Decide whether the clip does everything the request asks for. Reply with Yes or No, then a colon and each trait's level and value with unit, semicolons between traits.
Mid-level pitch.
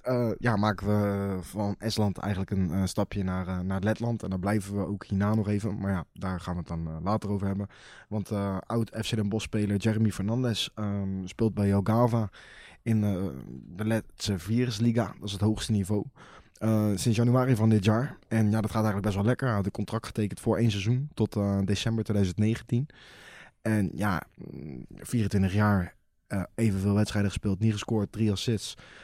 No: low, 105 Hz